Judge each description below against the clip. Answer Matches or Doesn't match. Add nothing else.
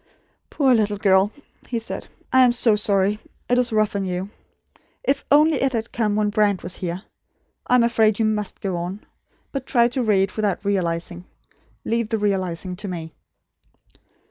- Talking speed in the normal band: Matches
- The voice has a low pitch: Doesn't match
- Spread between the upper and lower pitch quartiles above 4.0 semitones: Doesn't match